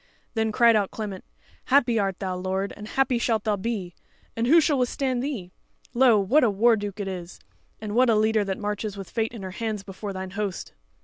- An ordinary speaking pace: No, fast, 210 wpm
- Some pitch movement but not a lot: Yes, average, 3.3 semitones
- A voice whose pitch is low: No, high, 215 Hz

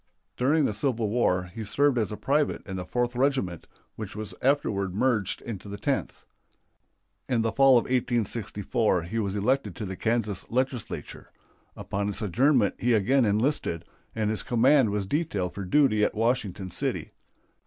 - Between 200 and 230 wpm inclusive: No, average, 165 wpm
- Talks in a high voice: No, low, 110 Hz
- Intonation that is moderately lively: Yes, average, 4.3 semitones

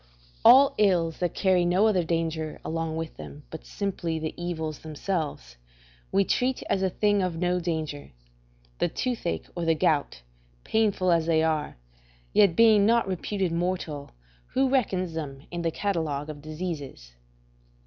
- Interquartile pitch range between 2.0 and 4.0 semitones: Yes, average, 3.5 semitones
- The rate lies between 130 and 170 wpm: Yes, average, 150 wpm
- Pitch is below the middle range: No, medium, 170 Hz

